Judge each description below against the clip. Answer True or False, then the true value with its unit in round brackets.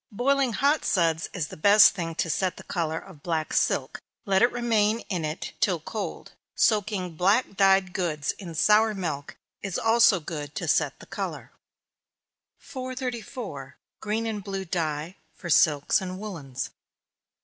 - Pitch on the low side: False (190 Hz)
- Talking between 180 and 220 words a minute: False (150 wpm)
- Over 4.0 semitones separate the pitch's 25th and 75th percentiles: True (4.9 semitones)